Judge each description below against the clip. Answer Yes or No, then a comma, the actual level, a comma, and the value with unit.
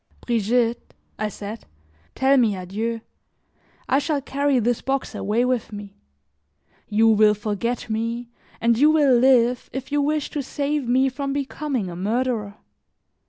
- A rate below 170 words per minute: Yes, average, 145 wpm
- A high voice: Yes, high, 240 Hz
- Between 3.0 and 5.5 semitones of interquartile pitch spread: Yes, average, 3.8 semitones